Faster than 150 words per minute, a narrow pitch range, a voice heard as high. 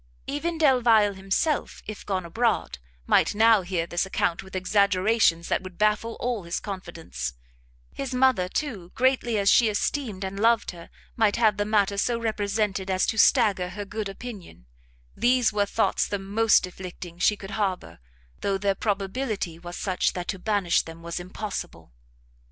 No: average, 165 wpm; average, 3.4 semitones; high, 200 Hz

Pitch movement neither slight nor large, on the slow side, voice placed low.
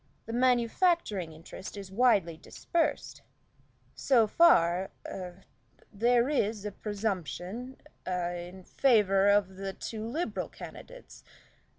No: average, 4.8 semitones; slow, 105 wpm; high, 205 Hz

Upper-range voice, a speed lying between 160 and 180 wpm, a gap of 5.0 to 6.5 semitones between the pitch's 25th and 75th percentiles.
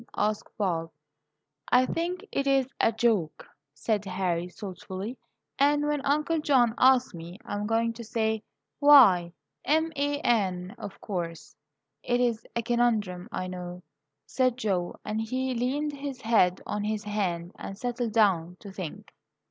No: high, 220 Hz; average, 150 wpm; wide, 5.6 semitones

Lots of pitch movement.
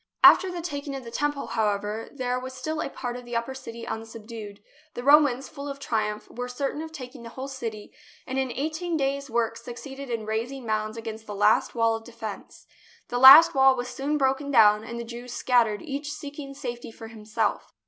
No: average, 3.6 semitones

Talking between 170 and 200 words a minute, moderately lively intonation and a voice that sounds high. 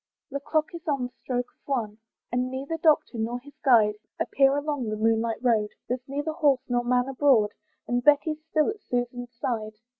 Yes: average, 185 wpm; average, 3.6 semitones; very high, 250 Hz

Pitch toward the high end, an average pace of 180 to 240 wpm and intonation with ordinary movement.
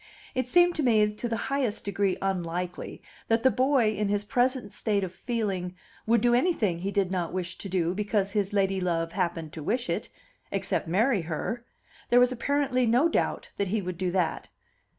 Yes: high, 205 Hz; average, 190 wpm; average, 5.0 semitones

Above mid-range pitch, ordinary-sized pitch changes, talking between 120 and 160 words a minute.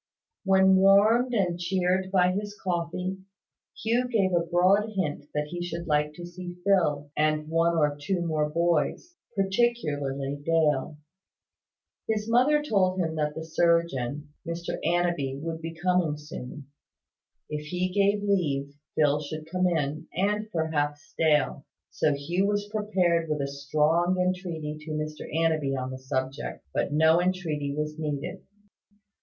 No: medium, 165 Hz; average, 3.8 semitones; average, 145 wpm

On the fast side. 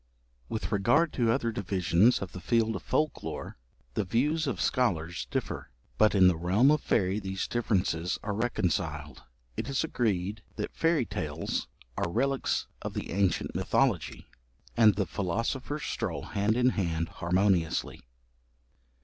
No: average, 145 wpm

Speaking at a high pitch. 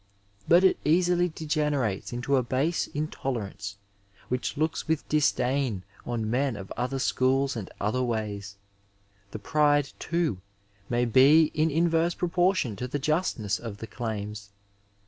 No: low, 130 Hz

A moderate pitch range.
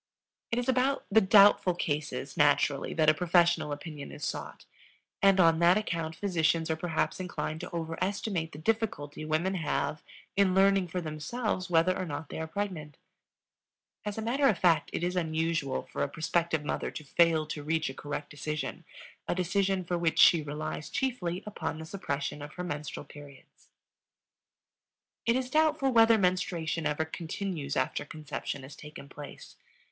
Yes: average, 4.0 semitones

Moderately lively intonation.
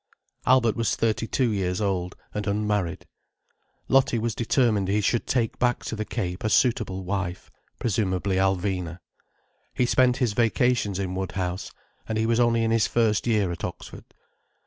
Yes: average, 3.5 semitones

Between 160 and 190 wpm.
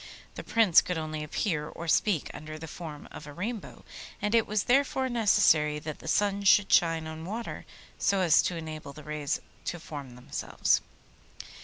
Yes: average, 175 wpm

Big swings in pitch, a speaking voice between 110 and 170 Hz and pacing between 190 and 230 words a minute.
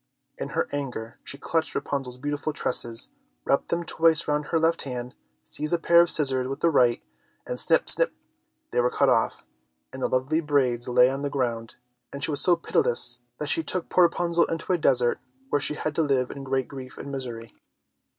No: average, 4.3 semitones; medium, 140 Hz; average, 200 wpm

